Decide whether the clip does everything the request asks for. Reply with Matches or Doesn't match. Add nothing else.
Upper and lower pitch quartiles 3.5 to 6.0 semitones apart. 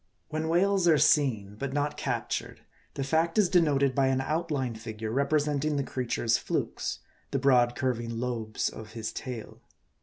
Matches